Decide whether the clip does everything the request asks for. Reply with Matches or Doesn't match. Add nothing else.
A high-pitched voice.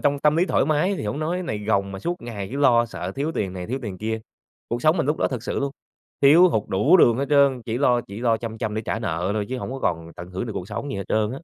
Doesn't match